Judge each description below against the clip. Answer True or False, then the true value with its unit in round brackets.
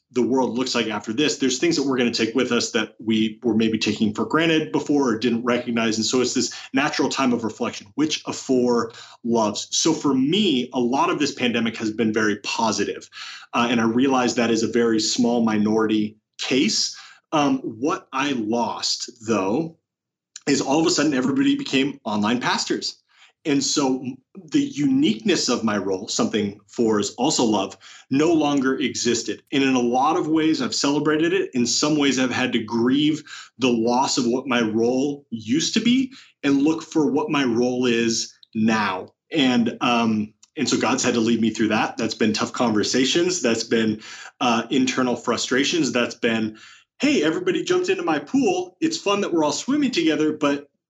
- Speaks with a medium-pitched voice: False (130 Hz)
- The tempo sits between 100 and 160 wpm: False (185 wpm)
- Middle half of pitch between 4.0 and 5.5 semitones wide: True (5.2 semitones)